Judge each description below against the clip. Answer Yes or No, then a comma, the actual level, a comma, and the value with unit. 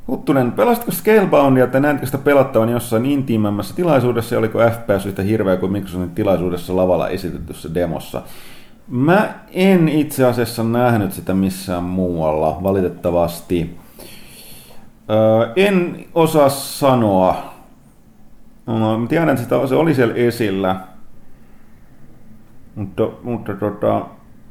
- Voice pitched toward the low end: Yes, low, 110 Hz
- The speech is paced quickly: No, average, 110 wpm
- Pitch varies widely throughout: Yes, wide, 6.3 semitones